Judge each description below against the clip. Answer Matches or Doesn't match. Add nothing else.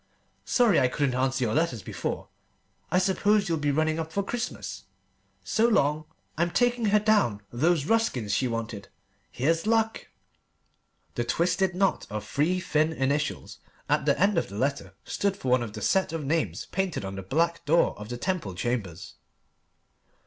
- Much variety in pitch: Matches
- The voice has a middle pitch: Matches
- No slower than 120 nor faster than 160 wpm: Doesn't match